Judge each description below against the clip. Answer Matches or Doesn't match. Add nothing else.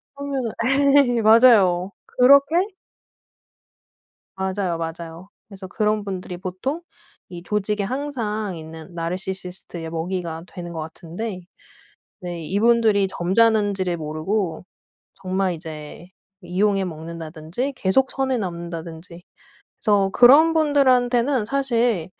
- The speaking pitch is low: Doesn't match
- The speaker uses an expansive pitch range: Doesn't match